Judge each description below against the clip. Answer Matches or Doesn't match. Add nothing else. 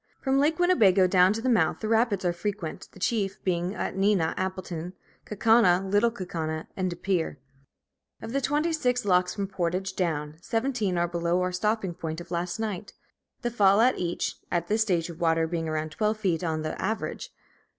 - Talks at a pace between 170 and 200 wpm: Matches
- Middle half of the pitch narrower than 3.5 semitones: Doesn't match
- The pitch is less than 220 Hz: Matches